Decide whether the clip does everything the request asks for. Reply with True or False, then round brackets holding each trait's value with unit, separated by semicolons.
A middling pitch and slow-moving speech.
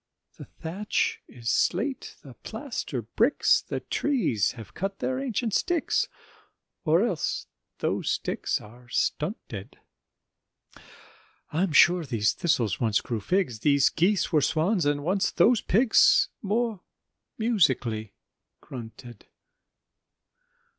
True (165 Hz; 110 wpm)